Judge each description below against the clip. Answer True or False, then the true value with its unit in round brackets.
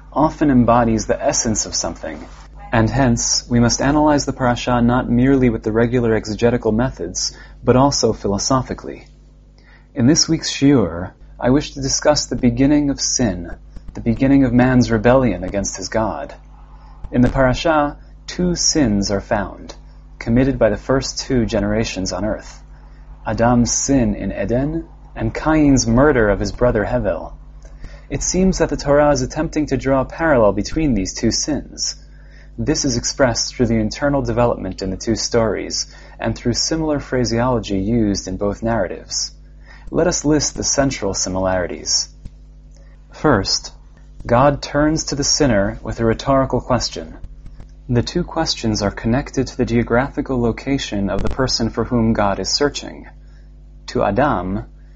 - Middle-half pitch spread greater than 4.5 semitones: False (3.8 semitones)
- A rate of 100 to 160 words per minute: True (150 wpm)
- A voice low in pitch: True (120 Hz)